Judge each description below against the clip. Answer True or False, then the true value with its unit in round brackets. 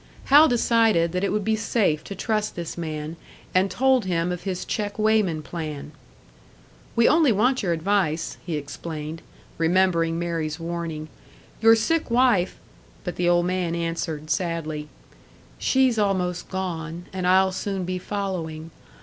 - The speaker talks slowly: False (150 wpm)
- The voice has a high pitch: False (180 Hz)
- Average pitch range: True (4.1 semitones)